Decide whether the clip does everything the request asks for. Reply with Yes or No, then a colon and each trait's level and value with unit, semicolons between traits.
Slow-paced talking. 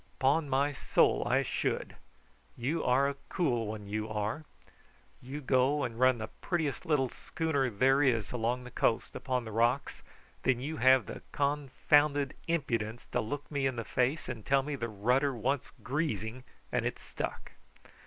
No: average, 170 wpm